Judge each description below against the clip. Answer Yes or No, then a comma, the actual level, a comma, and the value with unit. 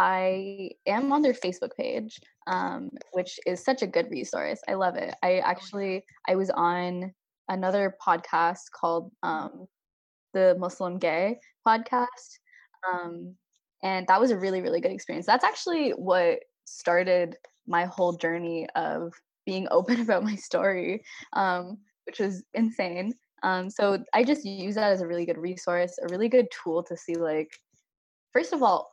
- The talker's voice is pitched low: No, high, 190 Hz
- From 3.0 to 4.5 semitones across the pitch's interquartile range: No, average, 5.0 semitones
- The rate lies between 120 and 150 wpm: No, average, 160 wpm